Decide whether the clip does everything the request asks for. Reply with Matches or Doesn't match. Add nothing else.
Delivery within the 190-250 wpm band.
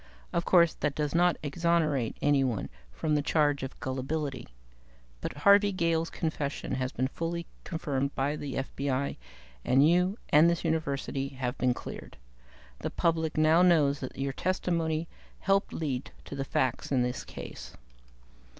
Doesn't match